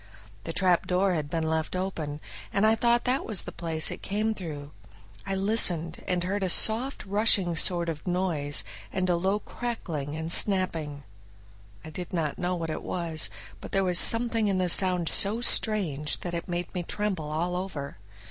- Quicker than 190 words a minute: No, average, 180 wpm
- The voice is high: No, medium, 180 Hz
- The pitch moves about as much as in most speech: Yes, average, 3.7 semitones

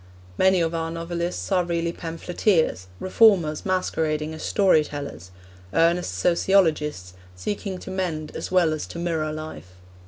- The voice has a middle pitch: Yes, medium, 165 Hz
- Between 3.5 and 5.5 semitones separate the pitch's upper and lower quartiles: No, average, 2.9 semitones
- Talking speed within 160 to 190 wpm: No, slow, 135 wpm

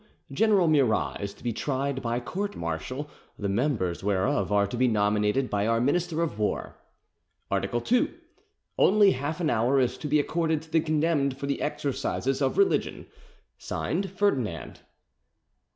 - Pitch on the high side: No, low, 135 Hz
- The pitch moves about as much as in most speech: No, wide, 5.7 semitones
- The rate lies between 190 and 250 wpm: No, average, 150 wpm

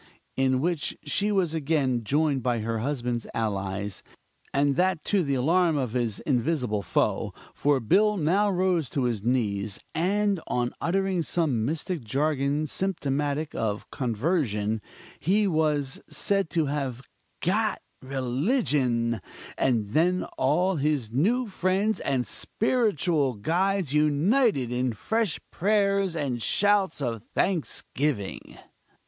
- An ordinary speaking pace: No, slow, 120 wpm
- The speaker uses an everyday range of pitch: No, wide, 6.9 semitones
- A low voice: No, medium, 145 Hz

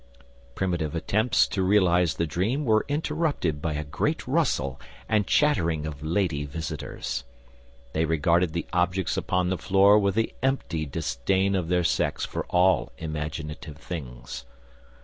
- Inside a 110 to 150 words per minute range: Yes, average, 140 wpm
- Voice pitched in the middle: No, very low, 85 Hz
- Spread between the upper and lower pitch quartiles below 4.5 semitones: Yes, average, 4.0 semitones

